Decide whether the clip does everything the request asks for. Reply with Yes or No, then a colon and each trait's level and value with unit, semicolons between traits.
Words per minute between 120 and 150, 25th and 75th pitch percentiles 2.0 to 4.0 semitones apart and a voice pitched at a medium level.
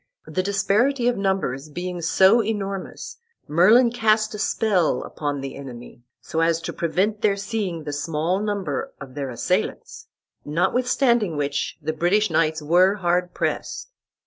No: average, 145 wpm; average, 5.3 semitones; medium, 180 Hz